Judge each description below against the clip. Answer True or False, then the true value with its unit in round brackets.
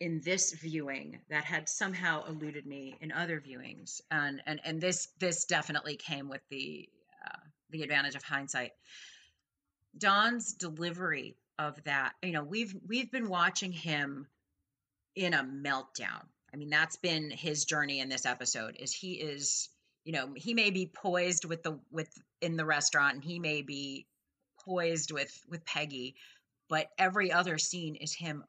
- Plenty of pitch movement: False (3.8 semitones)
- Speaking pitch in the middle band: True (155 Hz)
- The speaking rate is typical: True (160 wpm)